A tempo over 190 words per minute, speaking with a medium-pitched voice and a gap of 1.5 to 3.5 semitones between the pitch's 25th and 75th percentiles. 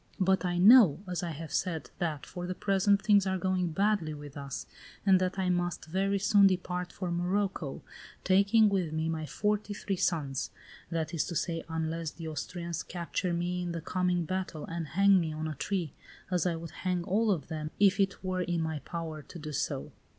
Yes: average, 200 wpm; medium, 175 Hz; average, 2.9 semitones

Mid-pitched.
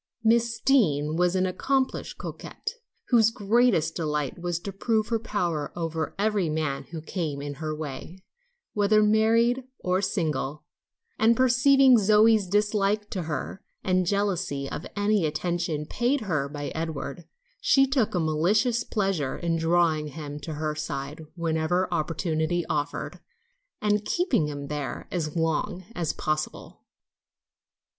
Yes: medium, 175 Hz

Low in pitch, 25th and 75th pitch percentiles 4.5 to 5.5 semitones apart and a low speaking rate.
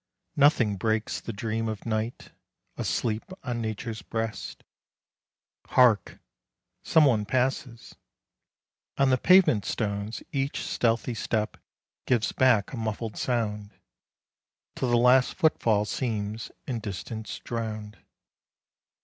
No: low, 115 Hz; narrow, 2.6 semitones; slow, 110 wpm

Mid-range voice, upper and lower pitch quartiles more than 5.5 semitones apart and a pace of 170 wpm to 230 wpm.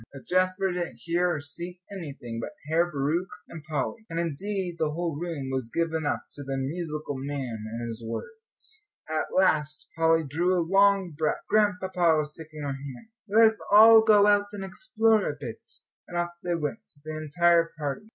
No: medium, 165 Hz; average, 4.3 semitones; average, 180 wpm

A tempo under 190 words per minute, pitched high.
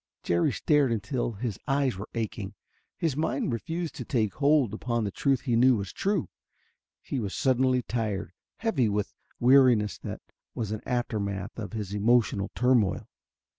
No: average, 155 wpm; low, 120 Hz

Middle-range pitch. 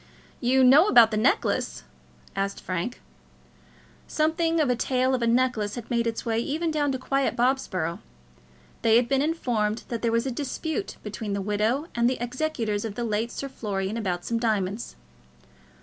No: high, 235 Hz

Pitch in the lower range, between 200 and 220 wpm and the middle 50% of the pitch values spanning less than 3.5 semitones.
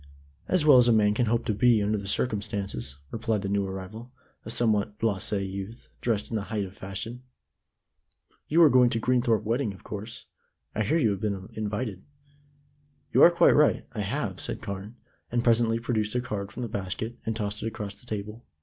Yes: low, 110 Hz; fast, 205 wpm; average, 2.8 semitones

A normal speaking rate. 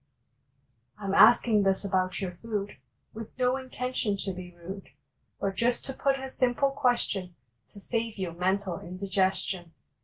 Yes: average, 150 wpm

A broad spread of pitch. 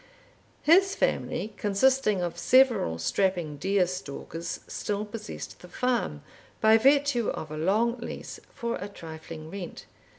Yes: wide, 5.8 semitones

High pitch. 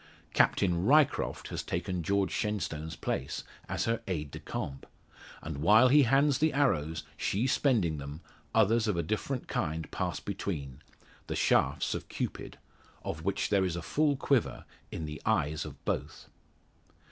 No: low, 100 Hz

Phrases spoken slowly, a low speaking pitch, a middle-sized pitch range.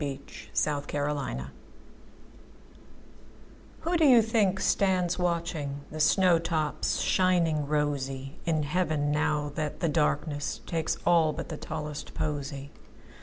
No: slow, 105 wpm; medium, 155 Hz; average, 3.1 semitones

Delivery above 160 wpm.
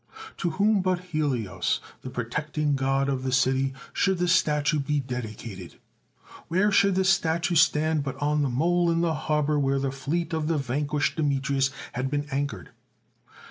Yes: average, 180 wpm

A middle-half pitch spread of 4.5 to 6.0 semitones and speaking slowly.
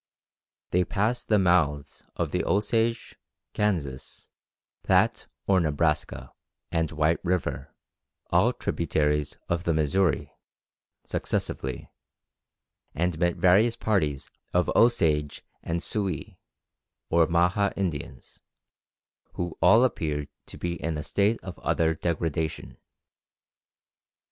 No: average, 4.1 semitones; slow, 105 wpm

